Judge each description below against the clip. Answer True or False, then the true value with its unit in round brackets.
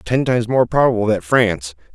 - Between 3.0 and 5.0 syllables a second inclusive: False (6.0 syllables/s)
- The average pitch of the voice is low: True (110 Hz)